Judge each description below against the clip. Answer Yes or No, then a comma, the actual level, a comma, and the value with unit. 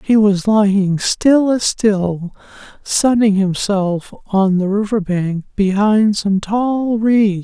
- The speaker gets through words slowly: Yes, slow, 130 wpm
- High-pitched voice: Yes, high, 205 Hz